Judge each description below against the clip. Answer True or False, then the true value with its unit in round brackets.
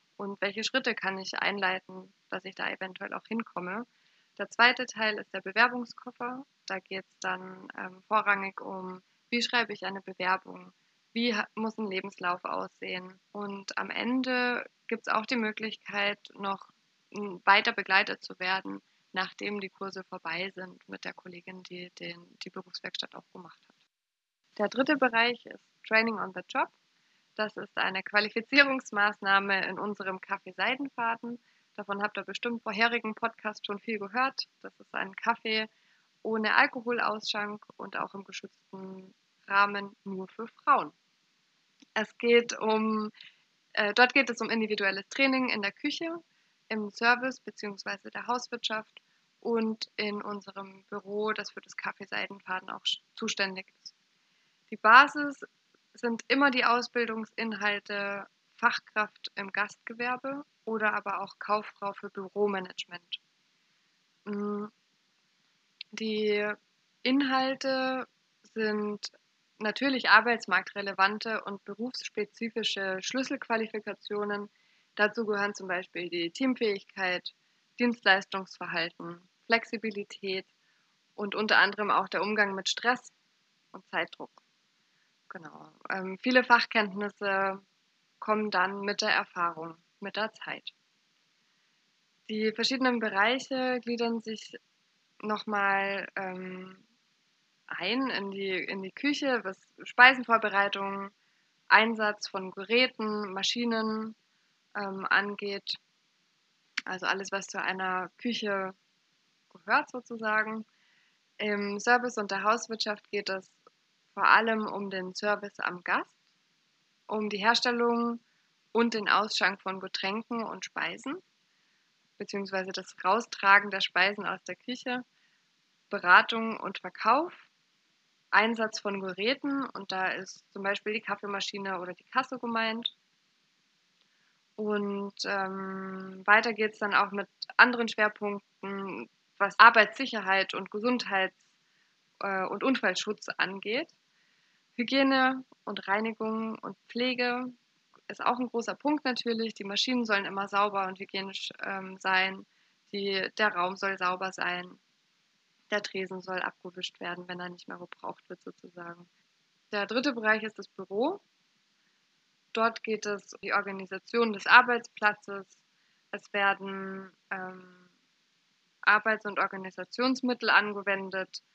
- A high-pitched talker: True (205 Hz)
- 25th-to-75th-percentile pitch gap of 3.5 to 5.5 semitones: False (3.0 semitones)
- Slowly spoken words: True (120 wpm)